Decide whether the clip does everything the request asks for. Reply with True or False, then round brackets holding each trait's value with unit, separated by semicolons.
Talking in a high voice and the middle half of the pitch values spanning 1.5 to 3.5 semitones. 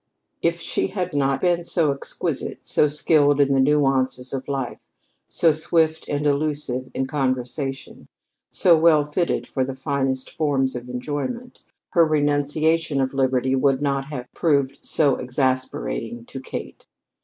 False (140 Hz; 2.7 semitones)